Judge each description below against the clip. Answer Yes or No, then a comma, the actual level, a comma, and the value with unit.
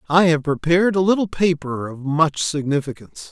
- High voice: No, medium, 160 Hz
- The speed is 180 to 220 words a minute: No, average, 165 wpm